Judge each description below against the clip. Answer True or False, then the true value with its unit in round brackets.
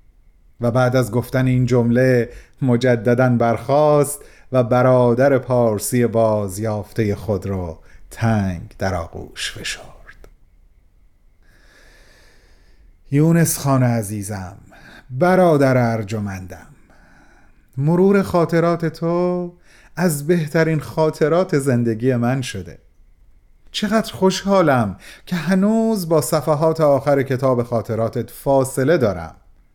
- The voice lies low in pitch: True (125 Hz)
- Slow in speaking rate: True (90 wpm)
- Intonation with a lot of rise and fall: True (6.7 semitones)